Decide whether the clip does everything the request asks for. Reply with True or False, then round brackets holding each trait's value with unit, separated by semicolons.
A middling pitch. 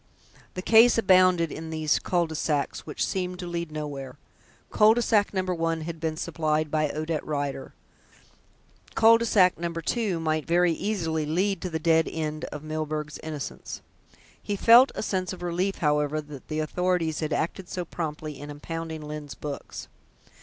True (160 Hz)